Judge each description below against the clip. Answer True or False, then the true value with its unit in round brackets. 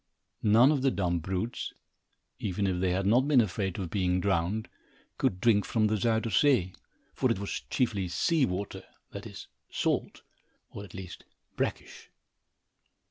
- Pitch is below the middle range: True (100 Hz)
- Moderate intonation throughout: True (3.8 semitones)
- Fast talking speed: False (155 wpm)